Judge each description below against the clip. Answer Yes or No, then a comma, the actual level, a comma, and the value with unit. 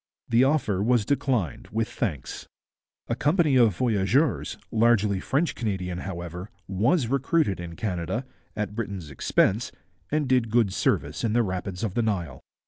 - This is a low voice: Yes, low, 110 Hz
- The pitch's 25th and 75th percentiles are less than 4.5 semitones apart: No, average, 5.0 semitones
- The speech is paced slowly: No, average, 145 wpm